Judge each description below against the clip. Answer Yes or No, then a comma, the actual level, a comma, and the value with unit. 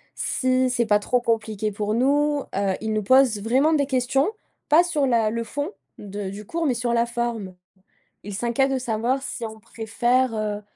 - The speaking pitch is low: No, high, 235 Hz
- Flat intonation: No, average, 3.7 semitones